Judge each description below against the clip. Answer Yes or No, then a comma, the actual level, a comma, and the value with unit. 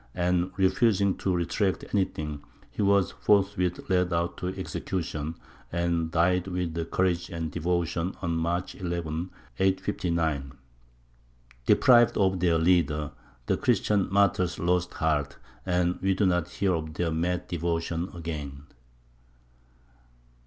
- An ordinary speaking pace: No, slow, 120 wpm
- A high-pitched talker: No, very low, 90 Hz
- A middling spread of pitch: No, narrow, 2.2 semitones